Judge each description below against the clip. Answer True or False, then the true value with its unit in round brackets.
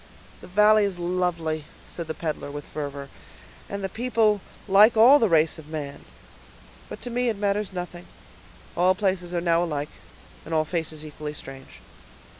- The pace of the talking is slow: False (165 wpm)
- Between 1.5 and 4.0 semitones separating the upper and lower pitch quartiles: False (4.6 semitones)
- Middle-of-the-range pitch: True (175 Hz)